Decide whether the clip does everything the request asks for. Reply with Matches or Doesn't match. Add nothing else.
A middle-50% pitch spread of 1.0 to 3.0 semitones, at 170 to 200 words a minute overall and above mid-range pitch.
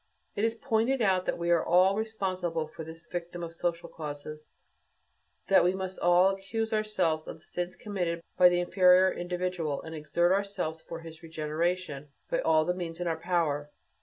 Doesn't match